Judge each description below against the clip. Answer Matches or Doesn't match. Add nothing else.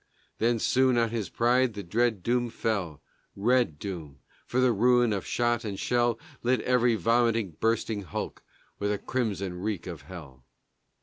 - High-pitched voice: Doesn't match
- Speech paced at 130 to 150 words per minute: Doesn't match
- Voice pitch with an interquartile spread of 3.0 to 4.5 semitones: Matches